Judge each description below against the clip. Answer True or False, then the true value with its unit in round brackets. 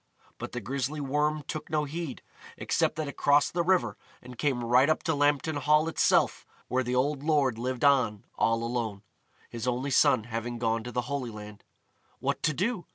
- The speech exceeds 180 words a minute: True (190 wpm)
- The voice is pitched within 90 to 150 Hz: True (135 Hz)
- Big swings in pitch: False (3.9 semitones)